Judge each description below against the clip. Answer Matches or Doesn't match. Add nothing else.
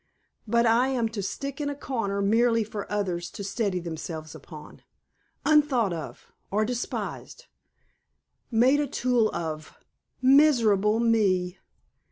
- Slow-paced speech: Matches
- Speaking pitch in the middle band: Doesn't match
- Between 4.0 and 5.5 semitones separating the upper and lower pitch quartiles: Matches